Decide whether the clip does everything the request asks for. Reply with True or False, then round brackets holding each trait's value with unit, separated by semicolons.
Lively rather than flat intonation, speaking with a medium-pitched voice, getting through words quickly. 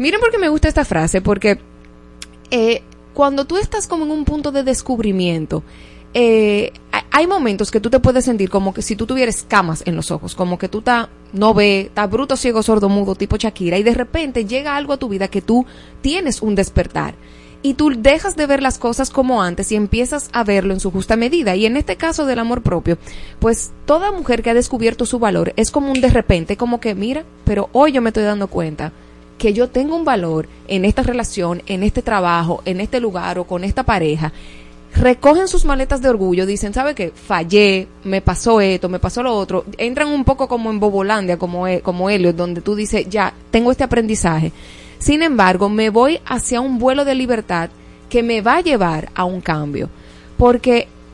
False (5.7 semitones; 220 Hz; 205 wpm)